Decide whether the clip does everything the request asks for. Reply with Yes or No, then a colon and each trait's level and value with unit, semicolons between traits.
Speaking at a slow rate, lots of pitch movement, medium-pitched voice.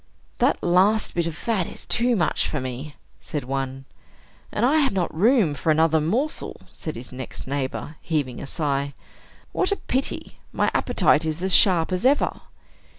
No: average, 170 wpm; wide, 7.0 semitones; medium, 160 Hz